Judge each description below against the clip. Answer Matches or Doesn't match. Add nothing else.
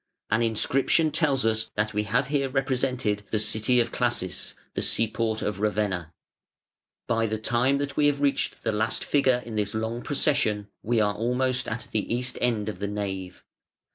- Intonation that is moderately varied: Matches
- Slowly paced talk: Doesn't match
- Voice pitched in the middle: Doesn't match